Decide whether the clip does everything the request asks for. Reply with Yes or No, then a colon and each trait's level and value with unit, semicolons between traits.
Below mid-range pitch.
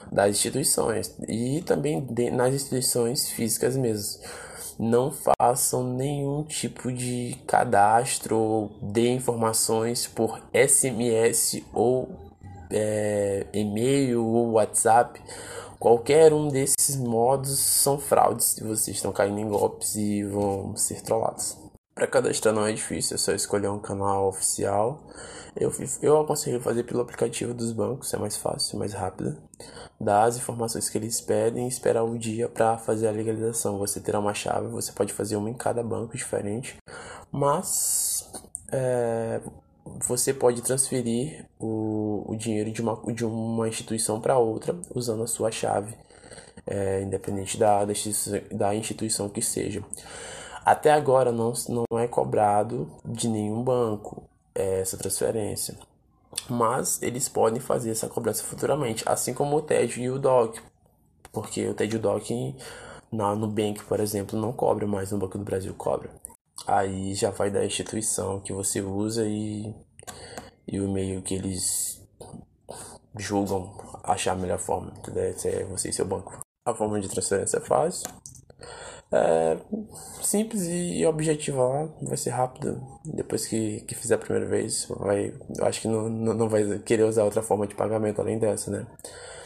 Yes: low, 110 Hz